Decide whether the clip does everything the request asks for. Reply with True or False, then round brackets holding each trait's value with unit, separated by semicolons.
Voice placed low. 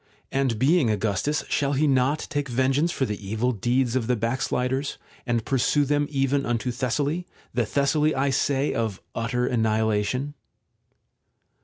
True (130 Hz)